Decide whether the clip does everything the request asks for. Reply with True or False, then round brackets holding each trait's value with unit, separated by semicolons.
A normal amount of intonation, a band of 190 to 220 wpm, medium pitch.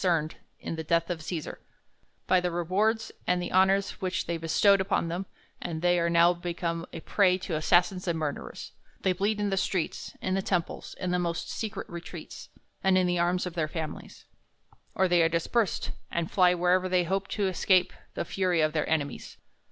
False (2.0 semitones; 195 wpm; 180 Hz)